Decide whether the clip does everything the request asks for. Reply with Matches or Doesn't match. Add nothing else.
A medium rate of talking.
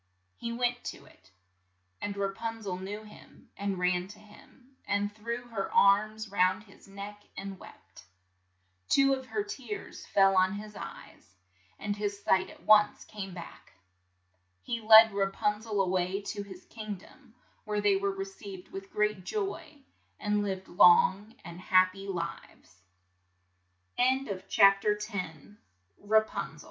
Doesn't match